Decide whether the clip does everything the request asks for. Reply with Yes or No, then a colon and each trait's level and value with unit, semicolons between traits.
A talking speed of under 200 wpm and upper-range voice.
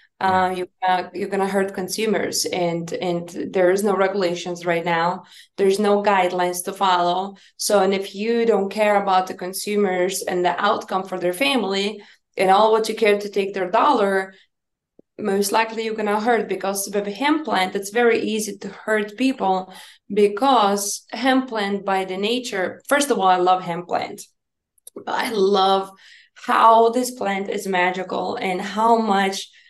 Yes: average, 170 wpm; high, 195 Hz